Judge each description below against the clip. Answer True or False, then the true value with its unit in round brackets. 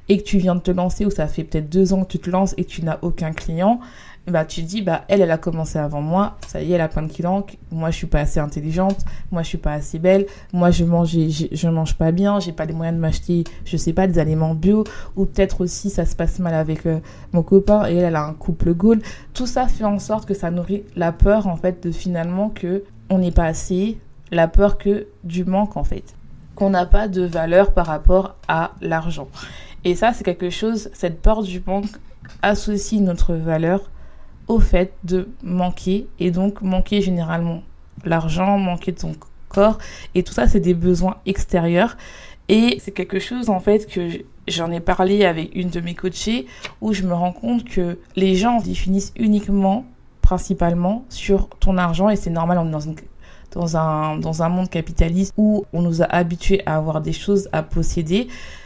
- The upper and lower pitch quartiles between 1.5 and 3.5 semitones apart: True (2.9 semitones)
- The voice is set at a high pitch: False (180 Hz)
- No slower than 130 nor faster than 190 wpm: False (215 wpm)